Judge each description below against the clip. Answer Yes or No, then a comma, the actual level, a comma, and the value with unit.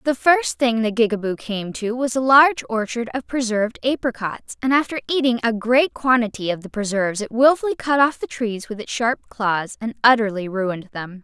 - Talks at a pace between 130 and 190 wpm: No, average, 200 wpm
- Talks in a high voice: Yes, high, 235 Hz